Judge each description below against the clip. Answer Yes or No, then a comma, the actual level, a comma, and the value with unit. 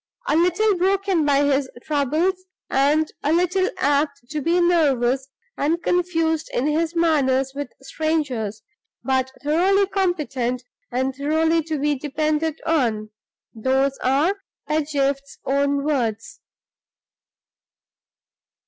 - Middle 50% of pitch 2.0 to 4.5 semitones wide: Yes, average, 3.5 semitones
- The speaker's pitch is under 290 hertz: No, very high, 295 Hz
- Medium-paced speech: No, slow, 110 wpm